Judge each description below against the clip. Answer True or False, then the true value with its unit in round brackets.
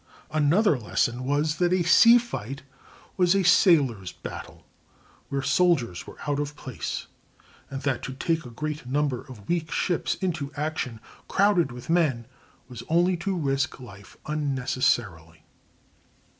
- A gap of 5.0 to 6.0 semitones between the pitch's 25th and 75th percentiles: True (5.4 semitones)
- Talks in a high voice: False (145 Hz)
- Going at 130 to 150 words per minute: True (140 wpm)